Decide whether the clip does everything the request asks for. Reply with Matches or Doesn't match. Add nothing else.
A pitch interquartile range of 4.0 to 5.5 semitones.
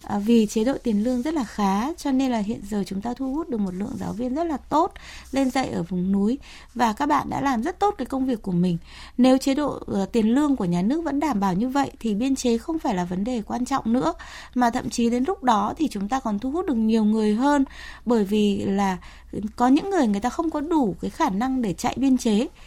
Matches